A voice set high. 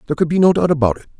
No: medium, 155 Hz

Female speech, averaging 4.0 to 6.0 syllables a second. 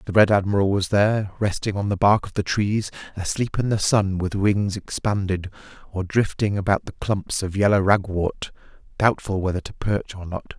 No: male; 5.0 syllables/s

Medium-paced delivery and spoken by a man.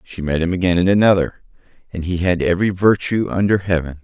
Yes: average, 180 wpm; male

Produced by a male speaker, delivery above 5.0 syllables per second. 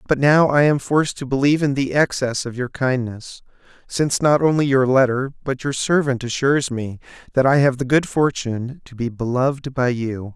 Yes: male; 5.3 syllables/s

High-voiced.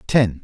No: low, 105 Hz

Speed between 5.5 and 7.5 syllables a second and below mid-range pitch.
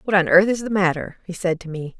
No: 6.0 syllables/s; medium, 185 Hz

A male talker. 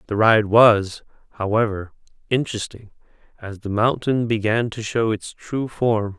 Yes: male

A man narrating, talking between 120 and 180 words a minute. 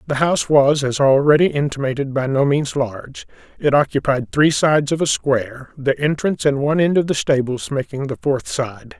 No: male; average, 195 wpm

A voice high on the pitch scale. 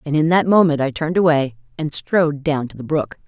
No: medium, 150 Hz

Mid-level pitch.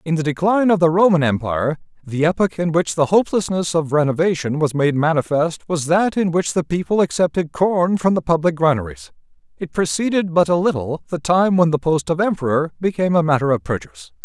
Yes: medium, 160 Hz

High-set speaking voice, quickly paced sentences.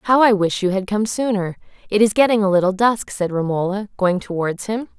Yes: high, 200 Hz; fast, 215 wpm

